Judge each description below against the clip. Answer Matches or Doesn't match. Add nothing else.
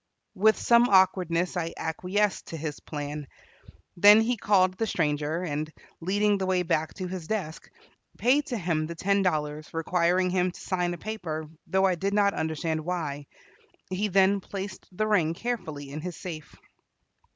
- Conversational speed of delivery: Matches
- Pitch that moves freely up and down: Doesn't match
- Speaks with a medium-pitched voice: Matches